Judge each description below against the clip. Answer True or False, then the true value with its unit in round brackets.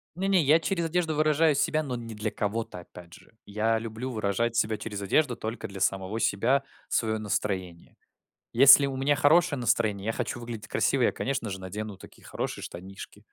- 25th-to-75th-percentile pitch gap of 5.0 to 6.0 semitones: True (5.3 semitones)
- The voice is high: False (115 Hz)